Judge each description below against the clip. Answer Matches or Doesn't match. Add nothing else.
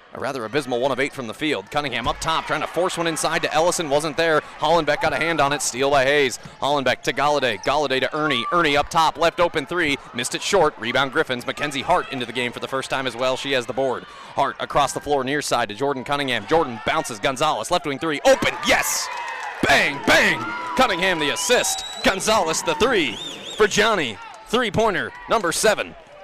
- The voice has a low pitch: Doesn't match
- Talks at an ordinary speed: Doesn't match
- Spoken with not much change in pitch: Doesn't match